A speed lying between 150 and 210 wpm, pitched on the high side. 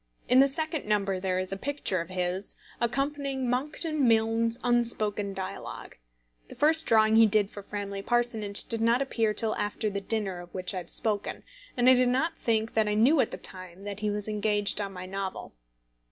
Yes: average, 195 wpm; high, 215 Hz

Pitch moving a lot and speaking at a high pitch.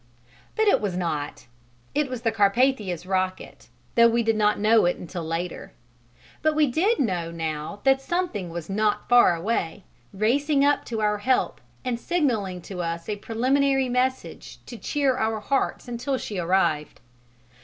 Yes: wide, 6.3 semitones; high, 220 Hz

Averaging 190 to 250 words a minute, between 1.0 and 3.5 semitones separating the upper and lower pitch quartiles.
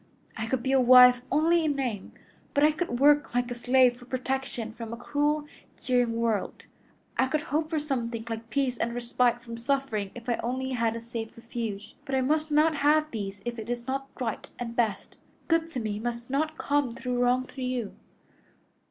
Yes: average, 200 wpm; average, 3.2 semitones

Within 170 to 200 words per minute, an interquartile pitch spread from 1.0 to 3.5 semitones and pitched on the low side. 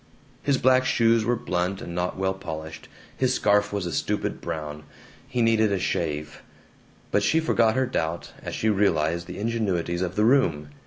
No: average, 175 wpm; average, 5.3 semitones; low, 100 Hz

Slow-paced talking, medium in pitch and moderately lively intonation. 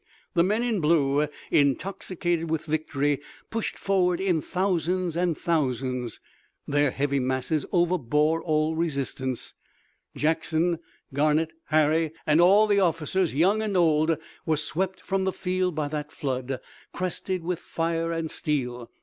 Yes: slow, 130 wpm; medium, 160 Hz; average, 3.5 semitones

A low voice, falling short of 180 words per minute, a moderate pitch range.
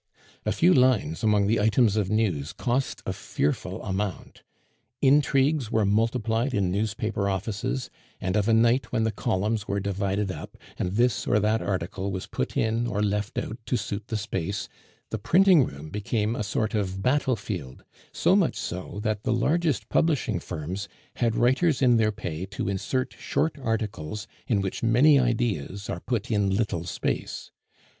Yes: low, 110 Hz; average, 165 wpm; average, 3.4 semitones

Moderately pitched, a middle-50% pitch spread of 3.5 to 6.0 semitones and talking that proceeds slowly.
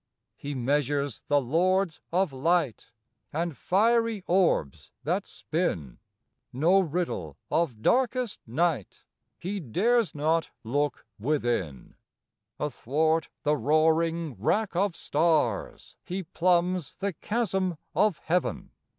Yes: medium, 165 Hz; average, 4.6 semitones; slow, 105 wpm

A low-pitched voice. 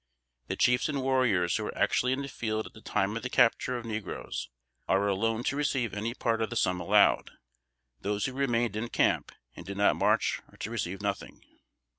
Yes: low, 115 Hz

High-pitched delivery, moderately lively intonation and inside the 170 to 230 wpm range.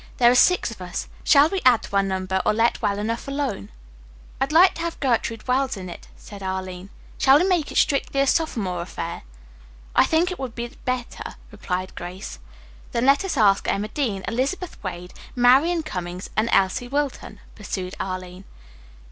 No: high, 230 Hz; wide, 6.6 semitones; average, 180 wpm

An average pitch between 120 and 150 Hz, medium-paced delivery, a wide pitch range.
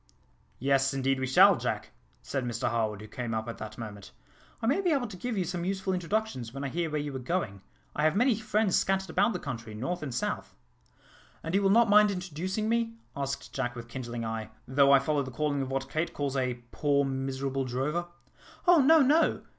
No: medium, 140 Hz; fast, 215 wpm; wide, 7.0 semitones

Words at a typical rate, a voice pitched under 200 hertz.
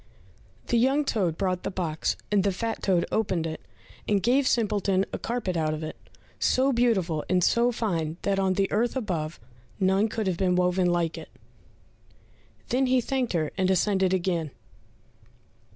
Yes: average, 170 wpm; high, 190 Hz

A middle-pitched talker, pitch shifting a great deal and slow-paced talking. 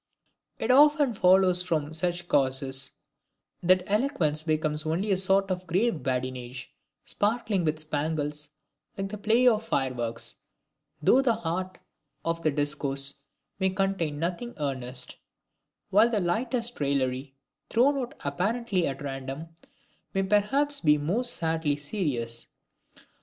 Yes: medium, 170 Hz; wide, 6.2 semitones; slow, 125 wpm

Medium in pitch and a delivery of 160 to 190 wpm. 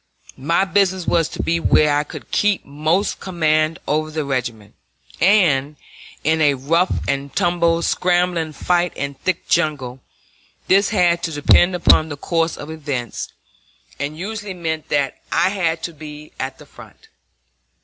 No: medium, 160 Hz; average, 150 wpm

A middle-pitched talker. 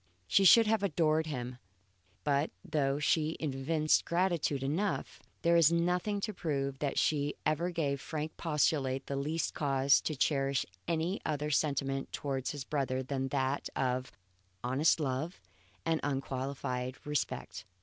Yes: medium, 145 Hz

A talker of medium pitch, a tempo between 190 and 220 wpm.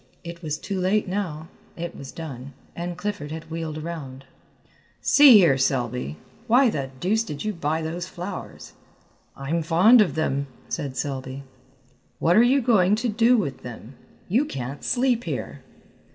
No: medium, 165 Hz; average, 155 wpm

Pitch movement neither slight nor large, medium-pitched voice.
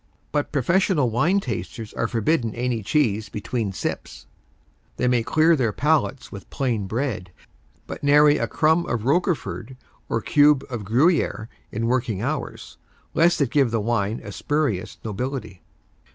No: average, 5.0 semitones; low, 125 Hz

